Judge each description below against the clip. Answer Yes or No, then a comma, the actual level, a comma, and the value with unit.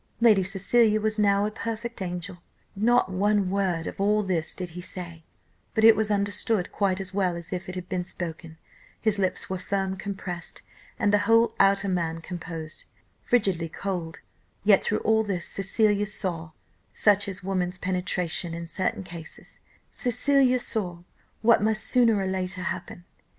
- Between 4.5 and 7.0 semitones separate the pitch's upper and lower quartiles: No, average, 2.9 semitones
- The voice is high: Yes, high, 195 Hz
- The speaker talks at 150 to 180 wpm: Yes, average, 160 wpm